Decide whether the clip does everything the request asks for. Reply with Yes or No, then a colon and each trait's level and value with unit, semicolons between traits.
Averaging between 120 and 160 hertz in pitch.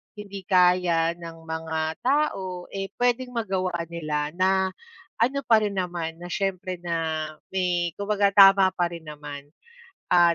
No: medium, 180 Hz